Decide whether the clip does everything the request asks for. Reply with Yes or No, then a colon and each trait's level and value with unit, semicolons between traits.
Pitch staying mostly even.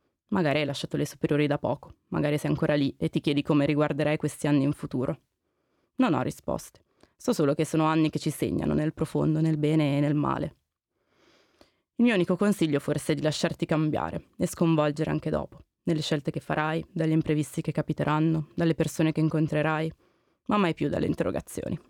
Yes: narrow, 1.2 semitones